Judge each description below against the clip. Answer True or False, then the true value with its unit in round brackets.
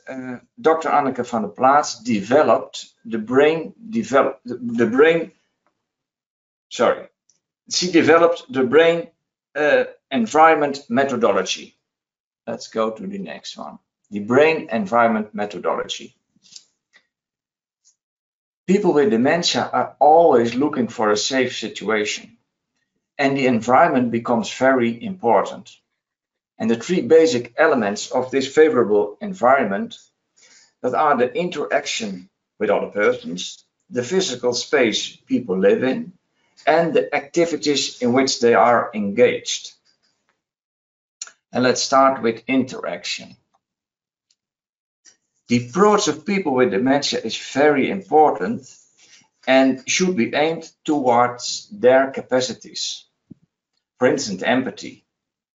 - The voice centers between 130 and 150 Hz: True (135 Hz)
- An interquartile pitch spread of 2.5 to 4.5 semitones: False (5.6 semitones)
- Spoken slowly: True (110 wpm)